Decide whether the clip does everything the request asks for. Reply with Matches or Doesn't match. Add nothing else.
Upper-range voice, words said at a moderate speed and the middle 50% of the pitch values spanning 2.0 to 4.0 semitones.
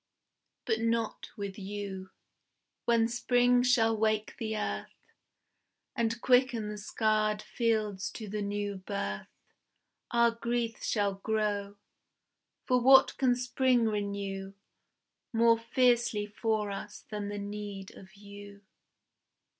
Doesn't match